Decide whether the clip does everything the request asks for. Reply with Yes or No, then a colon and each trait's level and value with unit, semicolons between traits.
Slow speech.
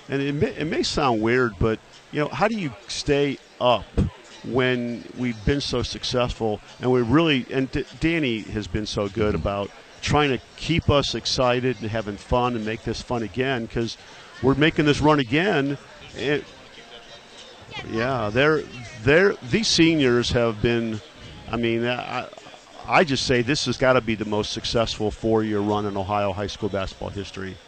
No: average, 175 wpm